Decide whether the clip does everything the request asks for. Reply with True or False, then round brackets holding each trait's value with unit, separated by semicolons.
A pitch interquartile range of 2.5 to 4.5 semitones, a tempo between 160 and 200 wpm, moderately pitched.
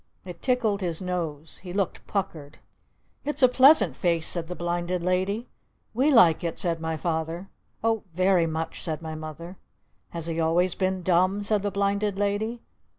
True (3.5 semitones; 165 wpm; 180 Hz)